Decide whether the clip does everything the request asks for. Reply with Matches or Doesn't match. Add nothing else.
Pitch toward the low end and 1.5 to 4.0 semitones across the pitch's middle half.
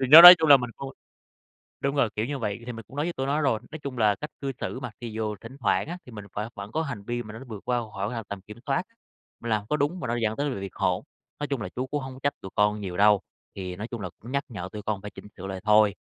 Doesn't match